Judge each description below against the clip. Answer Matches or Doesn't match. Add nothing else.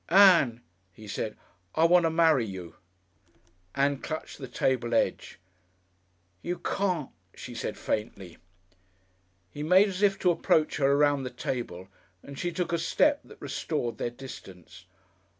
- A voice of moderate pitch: Matches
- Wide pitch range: Matches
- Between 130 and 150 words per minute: Matches